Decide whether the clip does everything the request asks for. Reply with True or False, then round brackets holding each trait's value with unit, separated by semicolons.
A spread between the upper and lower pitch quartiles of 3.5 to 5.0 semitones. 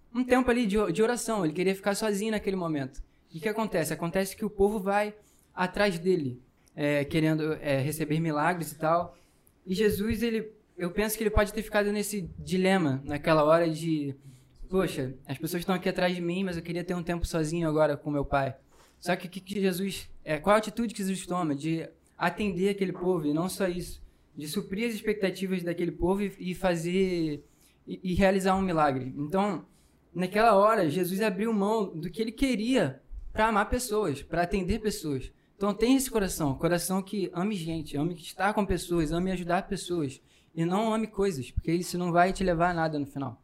True (4.3 semitones)